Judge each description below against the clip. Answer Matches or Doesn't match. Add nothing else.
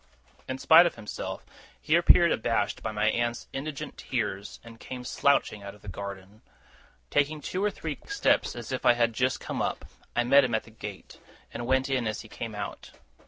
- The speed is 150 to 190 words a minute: Doesn't match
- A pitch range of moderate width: Matches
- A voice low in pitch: Matches